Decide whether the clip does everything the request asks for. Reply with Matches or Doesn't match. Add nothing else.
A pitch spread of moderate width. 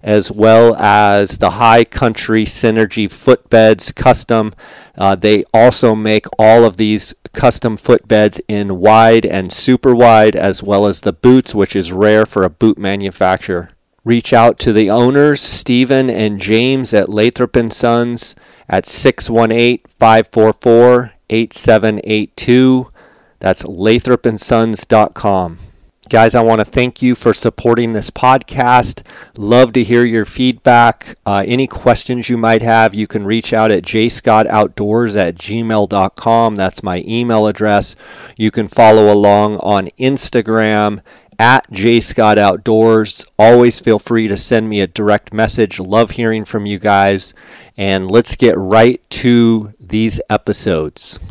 Doesn't match